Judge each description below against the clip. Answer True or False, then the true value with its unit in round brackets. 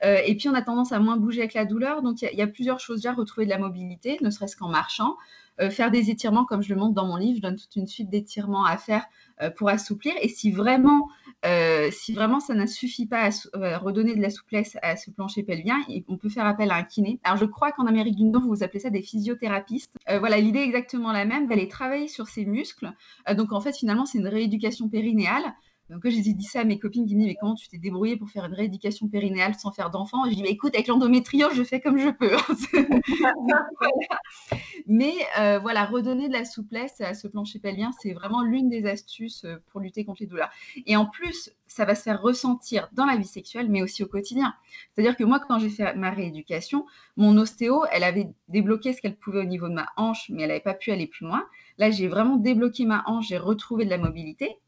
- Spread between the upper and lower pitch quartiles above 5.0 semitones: False (3.6 semitones)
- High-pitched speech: True (220 Hz)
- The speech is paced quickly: True (245 wpm)